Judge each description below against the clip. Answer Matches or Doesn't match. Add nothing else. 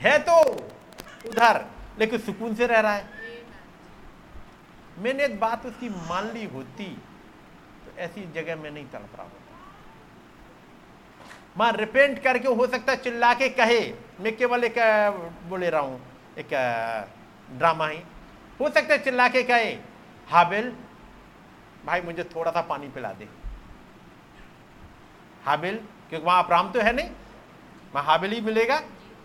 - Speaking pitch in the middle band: Doesn't match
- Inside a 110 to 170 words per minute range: Matches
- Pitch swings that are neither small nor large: Doesn't match